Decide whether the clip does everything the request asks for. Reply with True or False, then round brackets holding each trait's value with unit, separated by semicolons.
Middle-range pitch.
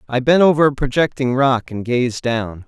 False (130 Hz)